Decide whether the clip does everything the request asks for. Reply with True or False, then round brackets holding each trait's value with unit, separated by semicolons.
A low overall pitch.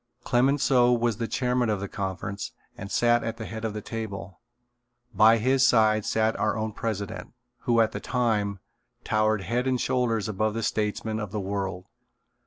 True (110 Hz)